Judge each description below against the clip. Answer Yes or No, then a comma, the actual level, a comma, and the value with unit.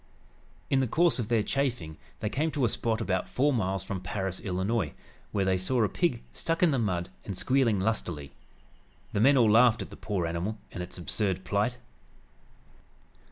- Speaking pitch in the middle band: No, low, 105 Hz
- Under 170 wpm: No, average, 185 wpm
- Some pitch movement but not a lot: Yes, average, 5.0 semitones